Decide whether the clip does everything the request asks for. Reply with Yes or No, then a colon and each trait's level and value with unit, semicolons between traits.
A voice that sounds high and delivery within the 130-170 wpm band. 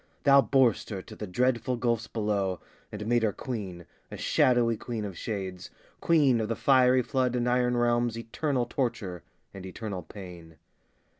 No: low, 115 Hz; average, 160 wpm